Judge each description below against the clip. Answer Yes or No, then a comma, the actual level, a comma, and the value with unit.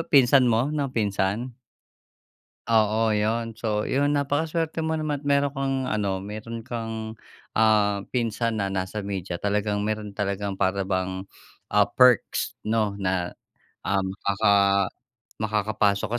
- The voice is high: No, low, 110 Hz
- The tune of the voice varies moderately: Yes, average, 3.3 semitones